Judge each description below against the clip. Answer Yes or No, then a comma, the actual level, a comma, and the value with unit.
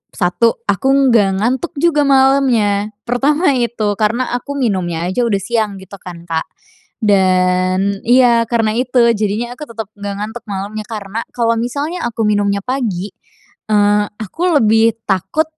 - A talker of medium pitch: No, high, 220 Hz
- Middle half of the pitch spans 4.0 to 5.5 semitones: No, average, 3.6 semitones